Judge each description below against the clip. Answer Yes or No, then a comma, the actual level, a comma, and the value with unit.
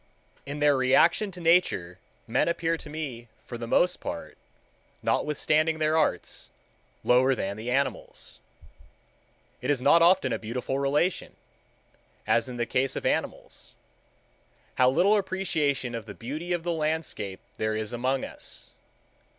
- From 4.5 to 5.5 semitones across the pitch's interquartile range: Yes, average, 5.1 semitones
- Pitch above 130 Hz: Yes, medium, 140 Hz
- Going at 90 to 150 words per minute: Yes, average, 145 wpm